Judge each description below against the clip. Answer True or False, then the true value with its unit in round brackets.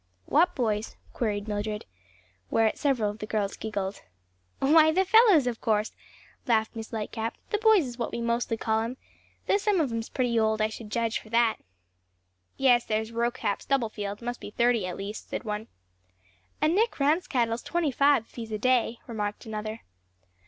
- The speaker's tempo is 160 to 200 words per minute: True (175 wpm)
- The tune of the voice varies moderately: True (3.4 semitones)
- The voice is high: True (230 Hz)